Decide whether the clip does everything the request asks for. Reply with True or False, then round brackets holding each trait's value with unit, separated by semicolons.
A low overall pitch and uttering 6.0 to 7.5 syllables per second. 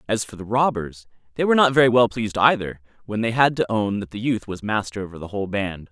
True (110 Hz; 6.4 syllables/s)